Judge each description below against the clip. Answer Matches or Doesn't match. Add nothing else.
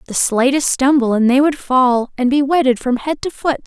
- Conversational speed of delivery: Doesn't match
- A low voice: Doesn't match